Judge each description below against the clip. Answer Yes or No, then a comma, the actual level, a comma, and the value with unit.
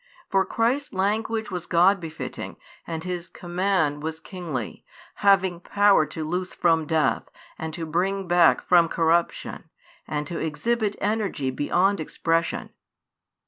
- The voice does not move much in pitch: No, average, 3.4 semitones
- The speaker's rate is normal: No, slow, 130 wpm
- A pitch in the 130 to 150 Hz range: No, medium, 175 Hz